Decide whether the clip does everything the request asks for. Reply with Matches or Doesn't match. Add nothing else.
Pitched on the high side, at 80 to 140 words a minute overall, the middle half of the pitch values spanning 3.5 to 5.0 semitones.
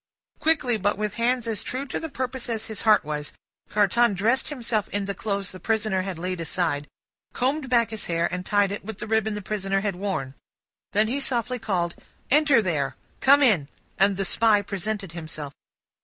Doesn't match